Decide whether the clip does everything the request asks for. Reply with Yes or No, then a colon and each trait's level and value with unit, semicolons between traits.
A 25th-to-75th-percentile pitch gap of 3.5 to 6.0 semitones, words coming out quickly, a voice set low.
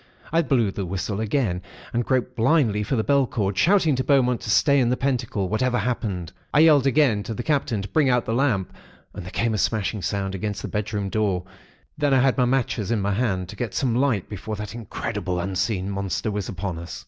Yes: average, 4.6 semitones; fast, 220 wpm; low, 110 Hz